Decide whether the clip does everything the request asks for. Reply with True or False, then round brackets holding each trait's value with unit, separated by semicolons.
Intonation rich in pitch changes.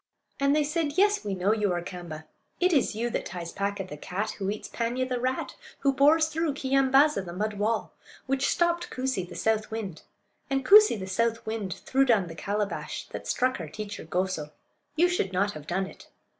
True (6.2 semitones)